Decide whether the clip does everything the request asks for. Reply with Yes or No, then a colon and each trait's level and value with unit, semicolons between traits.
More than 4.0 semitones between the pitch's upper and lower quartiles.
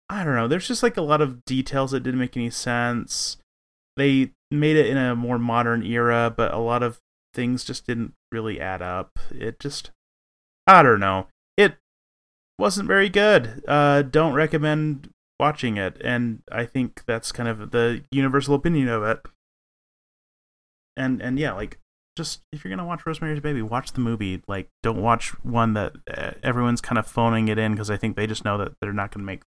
Yes: average, 4.5 semitones